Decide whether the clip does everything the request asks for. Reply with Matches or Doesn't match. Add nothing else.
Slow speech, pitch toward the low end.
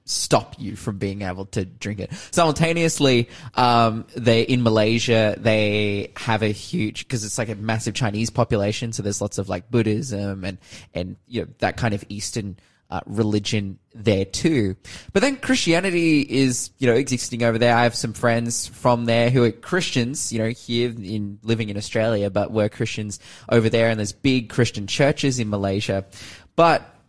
Doesn't match